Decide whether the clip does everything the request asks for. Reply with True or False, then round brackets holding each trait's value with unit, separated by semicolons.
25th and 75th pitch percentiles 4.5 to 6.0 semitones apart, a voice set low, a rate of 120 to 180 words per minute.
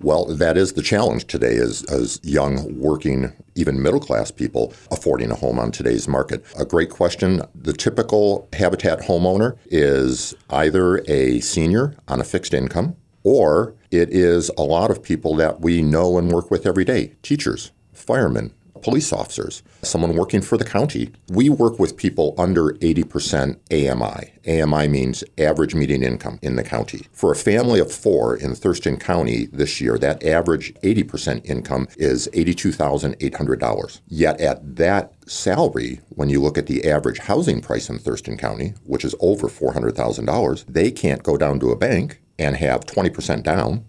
True (4.9 semitones; 85 Hz; 165 wpm)